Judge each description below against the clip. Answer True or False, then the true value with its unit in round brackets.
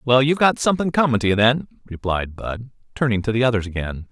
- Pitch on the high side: False (120 Hz)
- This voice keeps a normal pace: False (220 wpm)